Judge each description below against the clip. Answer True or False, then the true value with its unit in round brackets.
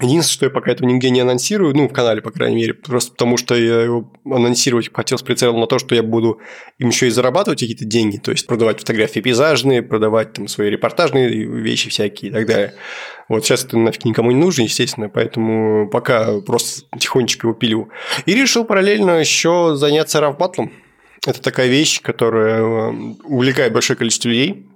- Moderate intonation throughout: True (3.5 semitones)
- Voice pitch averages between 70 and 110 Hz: False (120 Hz)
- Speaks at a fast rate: True (185 wpm)